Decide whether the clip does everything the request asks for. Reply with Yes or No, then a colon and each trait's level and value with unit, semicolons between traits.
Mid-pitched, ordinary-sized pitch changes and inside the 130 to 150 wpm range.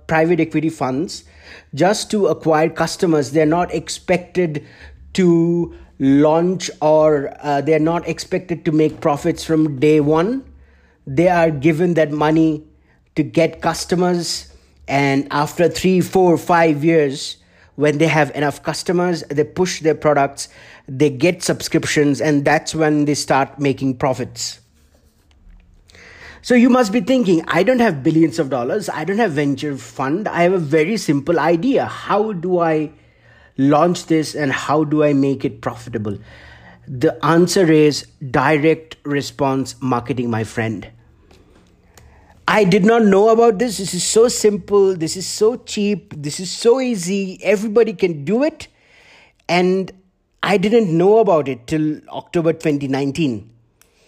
Yes: medium, 155 Hz; average, 4.2 semitones; average, 145 wpm